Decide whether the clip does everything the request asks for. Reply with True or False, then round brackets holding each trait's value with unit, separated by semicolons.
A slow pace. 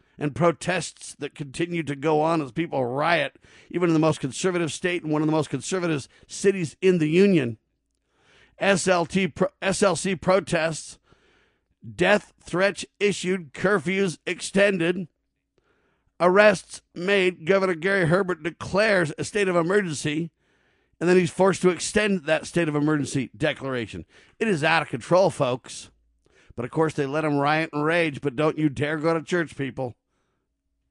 False (150 wpm)